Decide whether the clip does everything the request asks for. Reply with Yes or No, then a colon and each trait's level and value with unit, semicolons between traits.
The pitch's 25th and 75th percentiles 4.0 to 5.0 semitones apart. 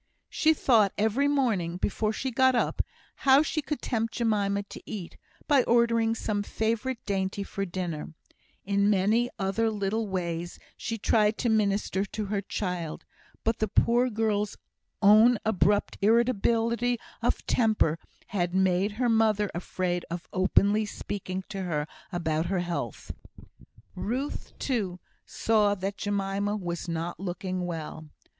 No: average, 3.4 semitones